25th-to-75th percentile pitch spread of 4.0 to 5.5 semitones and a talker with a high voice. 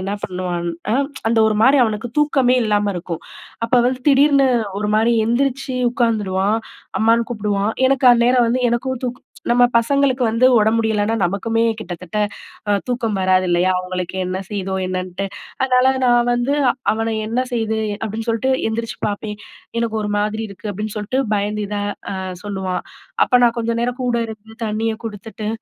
No: average, 3.1 semitones; high, 220 Hz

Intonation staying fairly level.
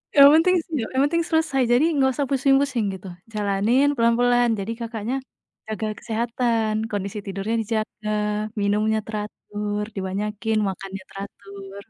No: average, 3.0 semitones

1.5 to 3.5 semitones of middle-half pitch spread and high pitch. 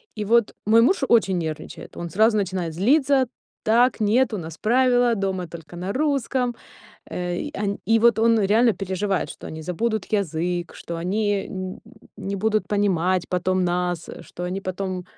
No: average, 4.2 semitones; high, 200 Hz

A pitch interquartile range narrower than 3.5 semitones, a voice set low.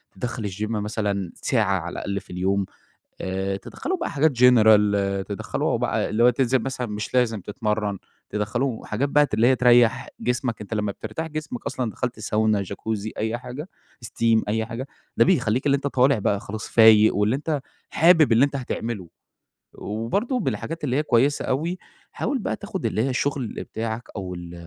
No: average, 4.2 semitones; low, 115 Hz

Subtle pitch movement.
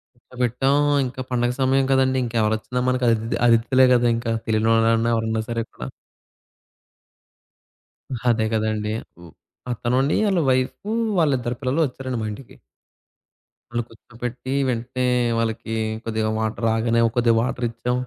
Yes: narrow, 2.1 semitones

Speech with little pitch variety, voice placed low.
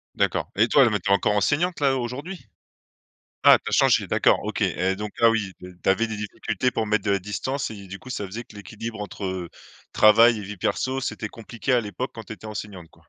No: average, 3.1 semitones; low, 110 Hz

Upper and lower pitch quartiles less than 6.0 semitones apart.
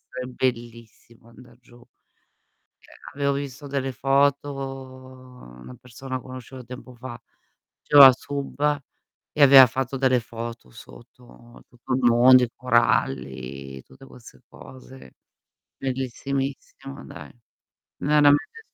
Yes: narrow, 2.5 semitones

